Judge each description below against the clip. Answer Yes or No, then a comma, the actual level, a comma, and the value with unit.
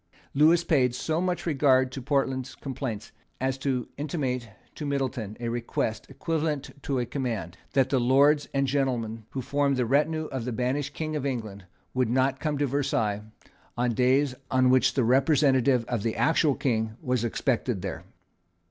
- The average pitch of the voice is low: Yes, low, 130 Hz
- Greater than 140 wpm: Yes, average, 165 wpm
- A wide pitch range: No, average, 2.9 semitones